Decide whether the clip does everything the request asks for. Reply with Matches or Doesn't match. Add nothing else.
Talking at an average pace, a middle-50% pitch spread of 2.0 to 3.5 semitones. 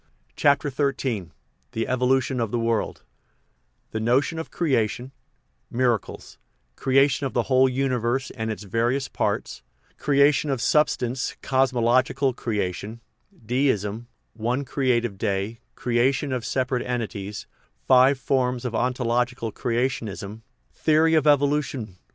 Doesn't match